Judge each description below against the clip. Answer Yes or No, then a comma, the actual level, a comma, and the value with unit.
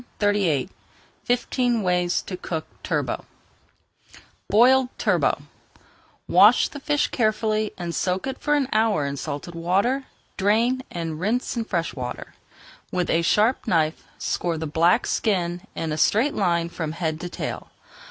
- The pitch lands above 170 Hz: Yes, medium, 185 Hz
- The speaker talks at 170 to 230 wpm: No, average, 145 wpm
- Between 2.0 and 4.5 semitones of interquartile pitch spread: No, wide, 5.4 semitones